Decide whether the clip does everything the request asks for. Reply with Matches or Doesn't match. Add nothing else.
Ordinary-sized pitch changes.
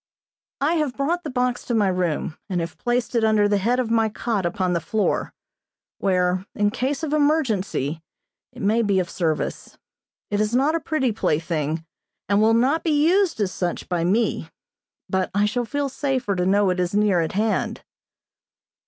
Doesn't match